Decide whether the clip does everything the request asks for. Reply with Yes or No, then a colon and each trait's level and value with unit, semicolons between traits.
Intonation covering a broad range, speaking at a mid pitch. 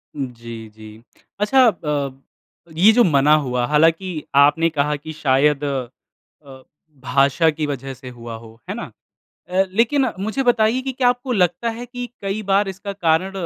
Yes: wide, 7.3 semitones; medium, 155 Hz